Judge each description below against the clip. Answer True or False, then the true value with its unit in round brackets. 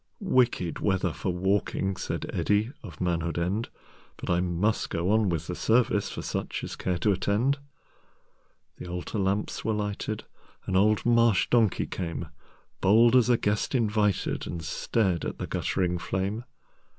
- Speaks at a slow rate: True (130 wpm)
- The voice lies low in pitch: True (100 Hz)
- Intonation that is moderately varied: True (3.8 semitones)